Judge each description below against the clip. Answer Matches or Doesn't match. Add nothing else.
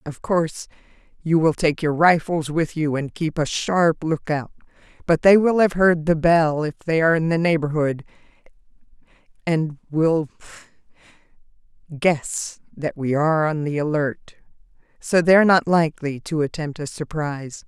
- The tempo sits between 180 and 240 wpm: Doesn't match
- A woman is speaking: Matches